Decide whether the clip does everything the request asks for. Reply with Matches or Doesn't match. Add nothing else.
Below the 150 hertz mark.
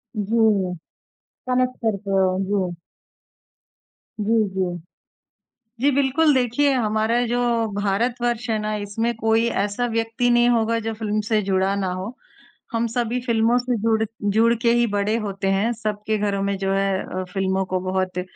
Doesn't match